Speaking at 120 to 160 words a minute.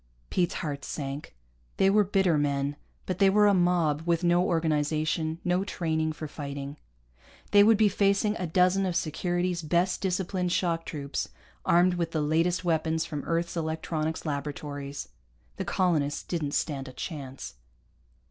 Yes: average, 150 wpm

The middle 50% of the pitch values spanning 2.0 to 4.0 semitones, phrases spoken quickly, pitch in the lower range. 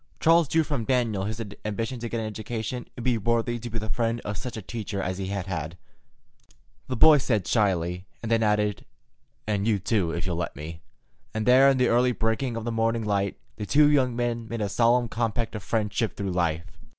Yes: average, 3.1 semitones; fast, 220 wpm; low, 115 Hz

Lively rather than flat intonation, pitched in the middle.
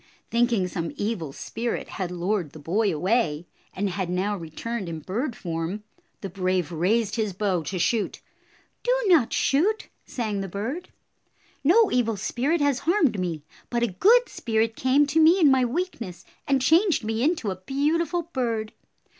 No: wide, 7.0 semitones; high, 225 Hz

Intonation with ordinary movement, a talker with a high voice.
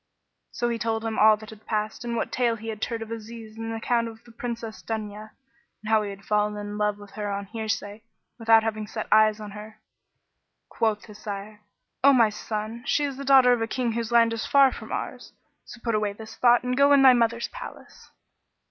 No: narrow, 1.7 semitones; high, 225 Hz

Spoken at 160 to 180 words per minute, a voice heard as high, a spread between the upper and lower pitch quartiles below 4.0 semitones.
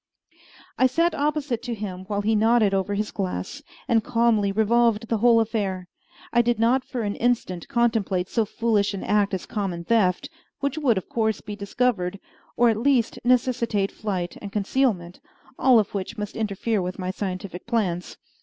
Yes: average, 175 wpm; high, 215 Hz; average, 3.3 semitones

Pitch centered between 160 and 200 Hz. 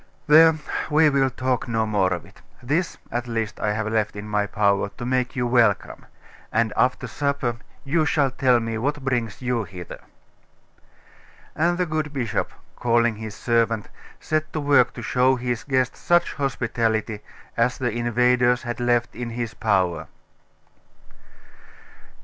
No: low, 120 Hz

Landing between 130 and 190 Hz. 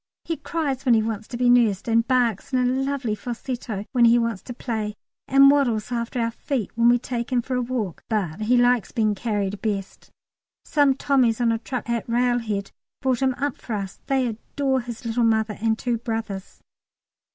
No: high, 235 Hz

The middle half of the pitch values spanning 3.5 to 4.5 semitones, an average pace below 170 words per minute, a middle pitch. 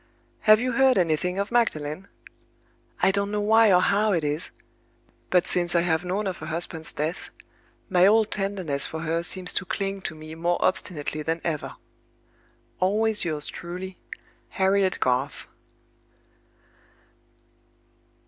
Yes: average, 3.9 semitones; average, 140 wpm; medium, 180 Hz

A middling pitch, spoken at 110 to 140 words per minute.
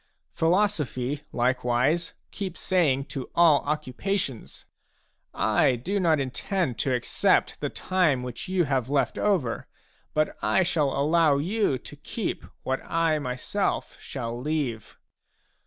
Yes: medium, 145 Hz; slow, 135 wpm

